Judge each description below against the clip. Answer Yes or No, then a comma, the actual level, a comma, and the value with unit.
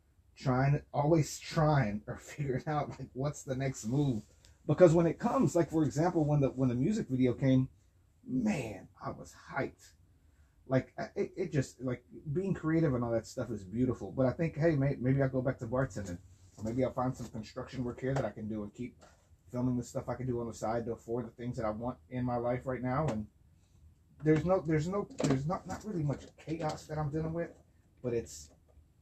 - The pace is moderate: No, fast, 215 wpm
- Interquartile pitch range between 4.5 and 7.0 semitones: Yes, average, 5.3 semitones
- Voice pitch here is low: Yes, low, 125 Hz